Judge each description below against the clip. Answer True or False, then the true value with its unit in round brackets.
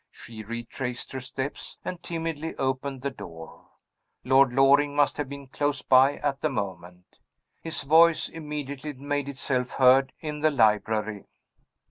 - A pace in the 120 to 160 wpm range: True (140 wpm)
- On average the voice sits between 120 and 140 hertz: True (135 Hz)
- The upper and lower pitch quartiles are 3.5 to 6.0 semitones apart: False (2.8 semitones)